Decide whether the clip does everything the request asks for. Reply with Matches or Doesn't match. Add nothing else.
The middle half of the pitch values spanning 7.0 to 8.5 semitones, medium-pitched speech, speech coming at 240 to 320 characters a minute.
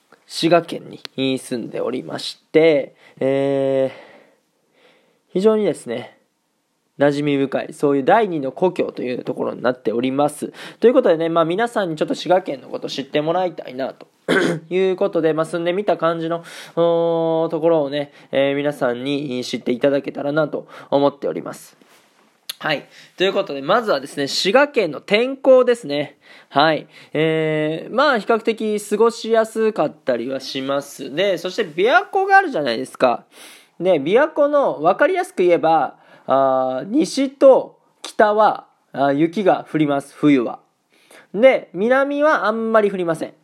Matches